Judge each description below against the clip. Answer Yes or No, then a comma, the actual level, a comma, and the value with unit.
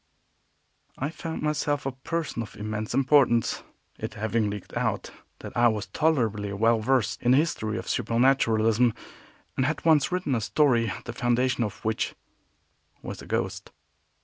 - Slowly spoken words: No, average, 150 wpm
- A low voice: Yes, low, 120 Hz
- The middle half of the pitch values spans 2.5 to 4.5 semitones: Yes, average, 4.2 semitones